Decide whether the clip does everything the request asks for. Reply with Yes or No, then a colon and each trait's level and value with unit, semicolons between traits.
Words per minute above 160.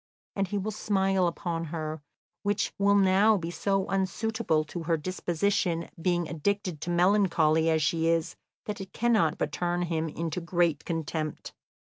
No: average, 155 wpm